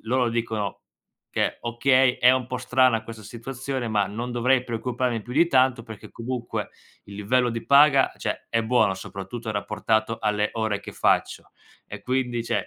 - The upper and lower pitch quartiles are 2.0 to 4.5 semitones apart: Yes, narrow, 2.5 semitones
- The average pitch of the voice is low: Yes, low, 120 Hz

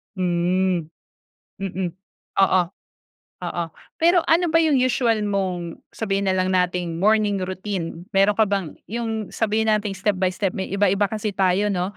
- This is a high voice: Yes, high, 195 Hz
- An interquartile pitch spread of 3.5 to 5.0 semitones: No, average, 2.7 semitones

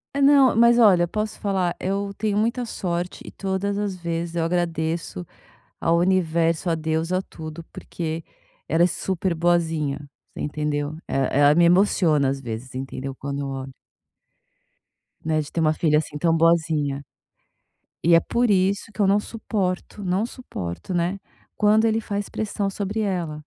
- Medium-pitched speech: Yes, medium, 170 Hz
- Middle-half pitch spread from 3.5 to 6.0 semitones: Yes, average, 4.3 semitones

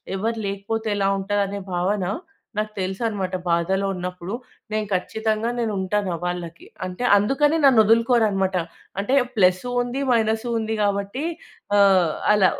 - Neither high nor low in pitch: No, high, 200 Hz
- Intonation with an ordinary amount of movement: Yes, average, 3.0 semitones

